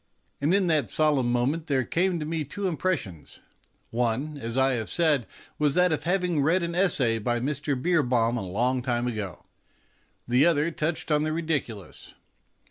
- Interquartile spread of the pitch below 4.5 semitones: No, average, 5.3 semitones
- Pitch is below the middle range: No, medium, 145 Hz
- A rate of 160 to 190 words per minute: Yes, average, 165 wpm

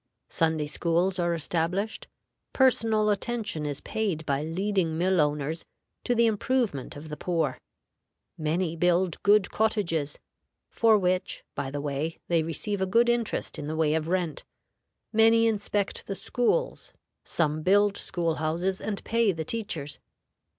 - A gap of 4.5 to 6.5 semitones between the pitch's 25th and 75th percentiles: Yes, average, 5.0 semitones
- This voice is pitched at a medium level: Yes, medium, 180 Hz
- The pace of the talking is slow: No, average, 145 wpm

